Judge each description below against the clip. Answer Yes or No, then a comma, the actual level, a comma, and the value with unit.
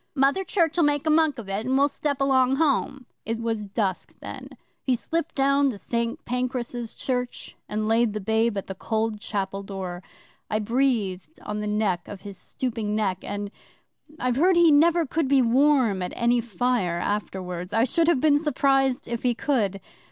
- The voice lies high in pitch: Yes, high, 235 Hz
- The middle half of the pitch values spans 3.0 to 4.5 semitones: No, average, 4.9 semitones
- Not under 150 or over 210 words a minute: Yes, average, 180 wpm